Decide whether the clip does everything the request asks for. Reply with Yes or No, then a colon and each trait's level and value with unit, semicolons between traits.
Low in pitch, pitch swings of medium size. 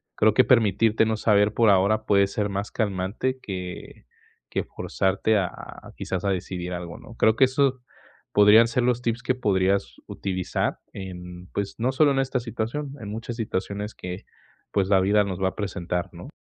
Yes: low, 105 Hz; average, 3.4 semitones